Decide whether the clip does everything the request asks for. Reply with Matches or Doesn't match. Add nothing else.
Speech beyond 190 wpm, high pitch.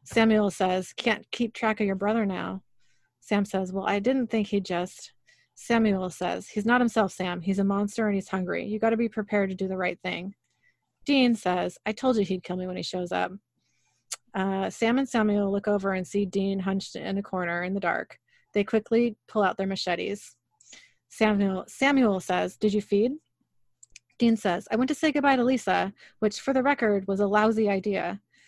Matches